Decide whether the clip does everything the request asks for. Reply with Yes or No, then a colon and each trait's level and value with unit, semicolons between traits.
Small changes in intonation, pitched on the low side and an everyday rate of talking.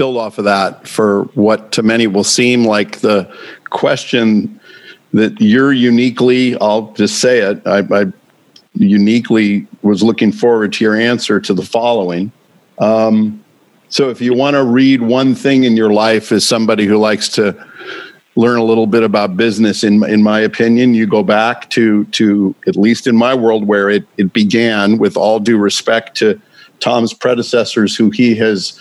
Yes: narrow, 2.2 semitones; low, 110 Hz; average, 175 wpm